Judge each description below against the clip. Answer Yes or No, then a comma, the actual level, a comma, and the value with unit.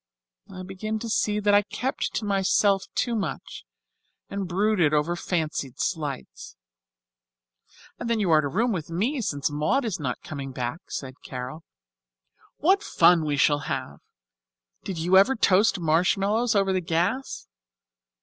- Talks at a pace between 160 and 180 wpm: No, average, 150 wpm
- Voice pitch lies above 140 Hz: Yes, medium, 185 Hz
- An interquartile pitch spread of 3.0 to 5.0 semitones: No, wide, 5.6 semitones